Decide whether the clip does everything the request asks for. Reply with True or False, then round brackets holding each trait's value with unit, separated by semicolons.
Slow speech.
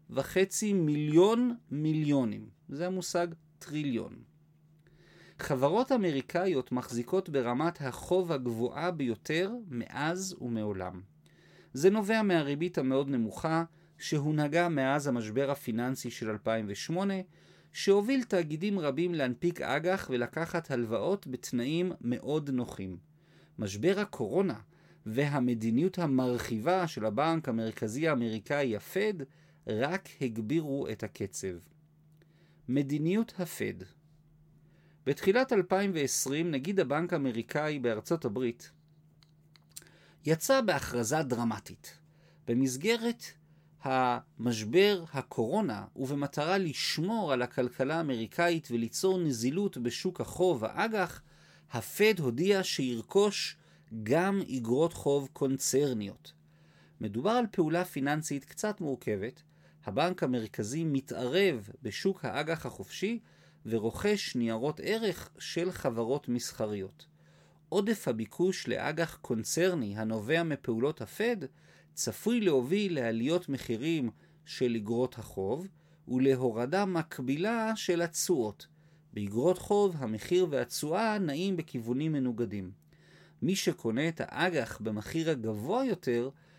True (90 wpm)